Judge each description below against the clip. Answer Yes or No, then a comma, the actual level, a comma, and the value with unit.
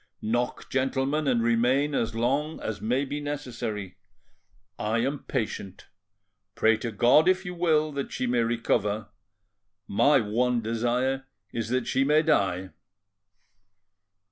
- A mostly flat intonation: No, average, 3.9 semitones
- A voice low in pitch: Yes, low, 125 Hz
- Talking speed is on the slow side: Yes, slow, 130 wpm